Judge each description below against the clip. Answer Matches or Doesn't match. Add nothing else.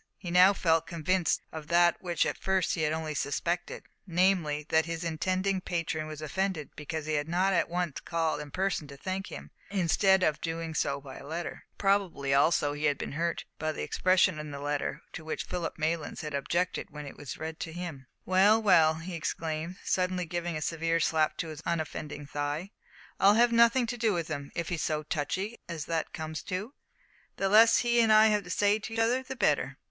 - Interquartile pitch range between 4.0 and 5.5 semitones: Doesn't match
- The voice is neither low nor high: Matches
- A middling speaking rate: Doesn't match